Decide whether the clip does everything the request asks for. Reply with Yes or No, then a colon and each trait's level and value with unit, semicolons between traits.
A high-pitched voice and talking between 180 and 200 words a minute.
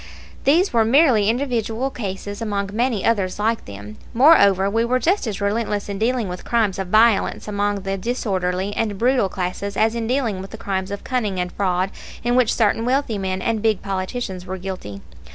Yes: high, 205 Hz; average, 190 wpm